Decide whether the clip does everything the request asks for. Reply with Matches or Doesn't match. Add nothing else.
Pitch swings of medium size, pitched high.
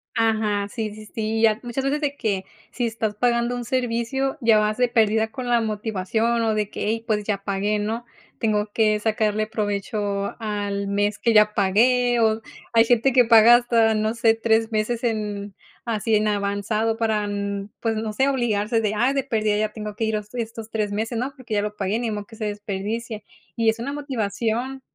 Doesn't match